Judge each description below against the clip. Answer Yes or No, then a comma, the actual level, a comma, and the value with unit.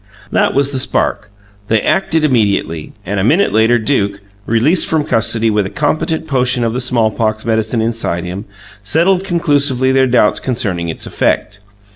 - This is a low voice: Yes, low, 115 Hz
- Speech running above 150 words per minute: Yes, average, 160 wpm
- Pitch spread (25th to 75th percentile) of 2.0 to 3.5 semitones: No, average, 5.2 semitones